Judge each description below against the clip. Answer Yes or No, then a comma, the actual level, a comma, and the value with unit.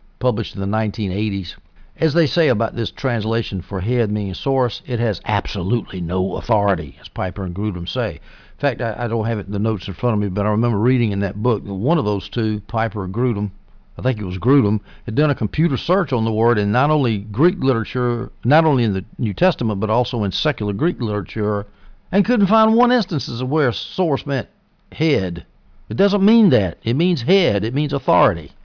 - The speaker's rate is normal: No, fast, 215 wpm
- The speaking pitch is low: Yes, low, 115 Hz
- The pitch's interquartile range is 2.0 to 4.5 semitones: No, average, 5.0 semitones